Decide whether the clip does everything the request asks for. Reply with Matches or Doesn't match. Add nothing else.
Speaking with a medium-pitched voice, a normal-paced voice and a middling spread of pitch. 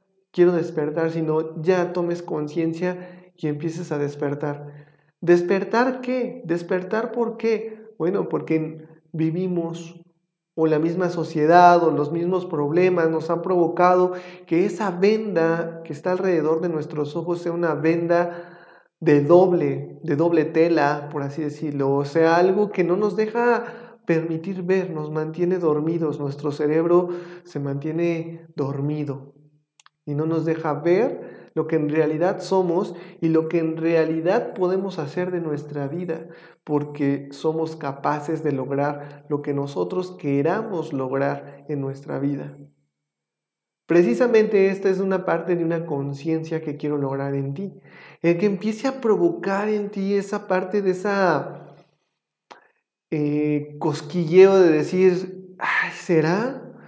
Matches